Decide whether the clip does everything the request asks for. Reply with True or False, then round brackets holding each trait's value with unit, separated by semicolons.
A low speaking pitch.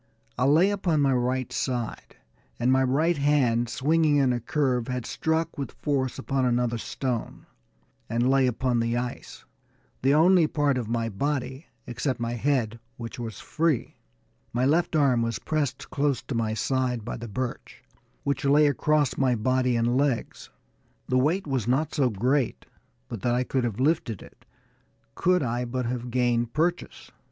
True (130 Hz)